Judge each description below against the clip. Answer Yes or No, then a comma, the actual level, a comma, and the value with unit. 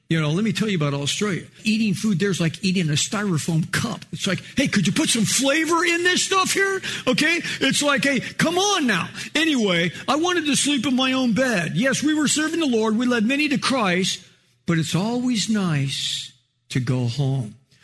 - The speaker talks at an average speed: No, fast, 210 wpm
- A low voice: No, high, 215 Hz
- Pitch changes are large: Yes, wide, 8.5 semitones